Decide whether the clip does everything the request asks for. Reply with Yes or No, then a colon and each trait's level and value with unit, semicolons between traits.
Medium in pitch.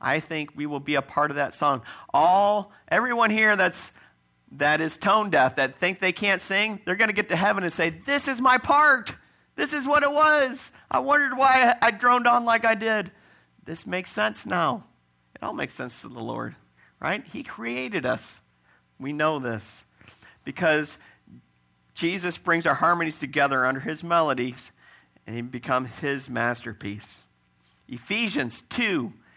Yes: medium, 160 Hz